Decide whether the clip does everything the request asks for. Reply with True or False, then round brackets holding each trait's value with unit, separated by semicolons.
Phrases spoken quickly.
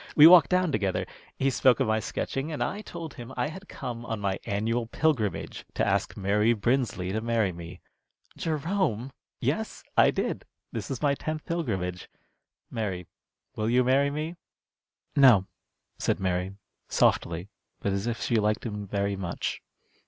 False (160 wpm)